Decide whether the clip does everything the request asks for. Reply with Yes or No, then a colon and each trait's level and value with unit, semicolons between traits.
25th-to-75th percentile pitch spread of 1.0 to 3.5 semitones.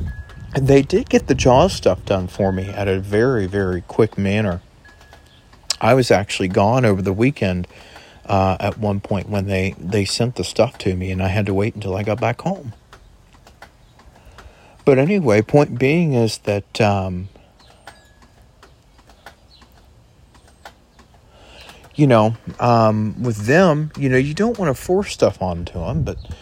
No: average, 4.2 semitones